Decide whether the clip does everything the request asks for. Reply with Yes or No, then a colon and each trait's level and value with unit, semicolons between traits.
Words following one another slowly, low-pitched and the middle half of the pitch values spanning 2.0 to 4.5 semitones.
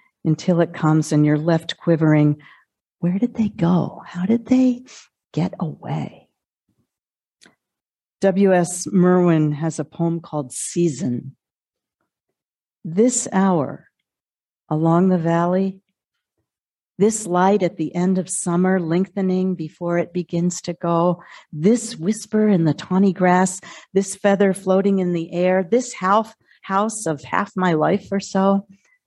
No: slow, 130 wpm; medium, 180 Hz; average, 2.7 semitones